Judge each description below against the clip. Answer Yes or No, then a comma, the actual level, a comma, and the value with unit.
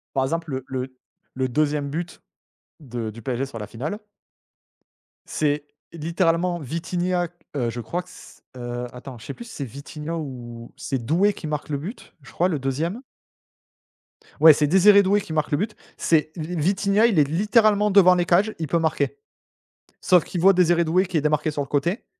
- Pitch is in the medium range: Yes, medium, 160 Hz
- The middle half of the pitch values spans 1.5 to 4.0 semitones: No, average, 4.7 semitones